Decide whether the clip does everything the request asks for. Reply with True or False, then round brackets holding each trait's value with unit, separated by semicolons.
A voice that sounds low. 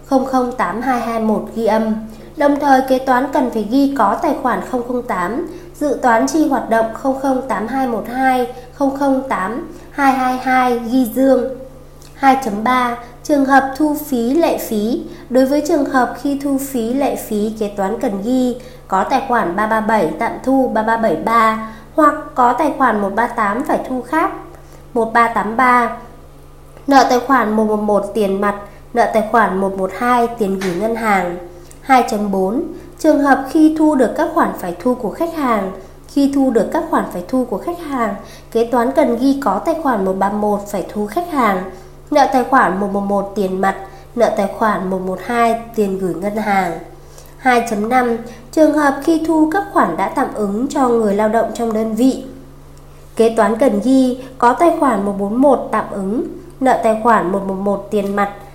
False (240 Hz)